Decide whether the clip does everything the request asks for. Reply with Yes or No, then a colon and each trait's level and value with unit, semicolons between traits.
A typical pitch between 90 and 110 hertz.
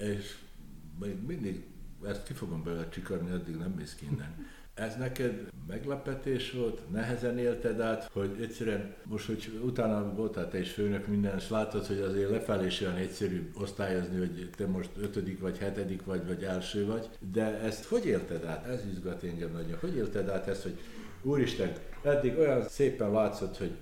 Yes: low, 100 Hz